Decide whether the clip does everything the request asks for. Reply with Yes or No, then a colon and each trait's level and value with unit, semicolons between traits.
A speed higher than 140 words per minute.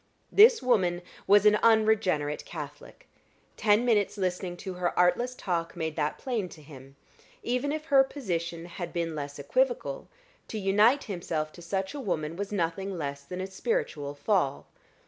Yes: average, 160 wpm